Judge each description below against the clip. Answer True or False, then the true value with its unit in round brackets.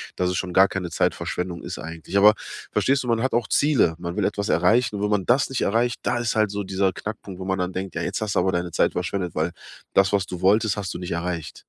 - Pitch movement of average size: True (3.3 semitones)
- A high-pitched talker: False (95 Hz)